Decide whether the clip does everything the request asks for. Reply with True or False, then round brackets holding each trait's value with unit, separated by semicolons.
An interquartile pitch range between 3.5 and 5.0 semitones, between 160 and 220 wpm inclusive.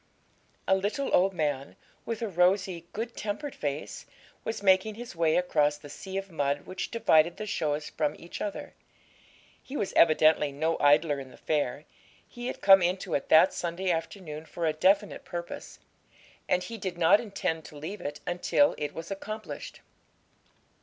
True (4.3 semitones; 165 wpm)